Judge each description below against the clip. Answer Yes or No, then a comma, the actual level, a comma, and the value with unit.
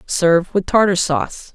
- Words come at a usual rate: Yes, average, 155 wpm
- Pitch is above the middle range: No, medium, 180 Hz